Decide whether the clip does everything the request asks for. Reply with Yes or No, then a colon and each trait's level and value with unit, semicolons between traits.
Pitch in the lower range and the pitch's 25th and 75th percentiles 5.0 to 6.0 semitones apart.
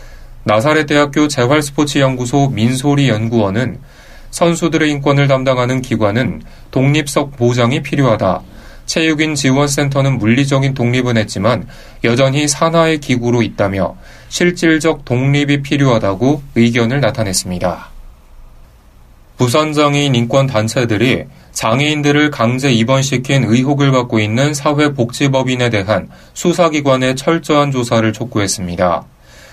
No: low, 130 Hz; average, 4.3 semitones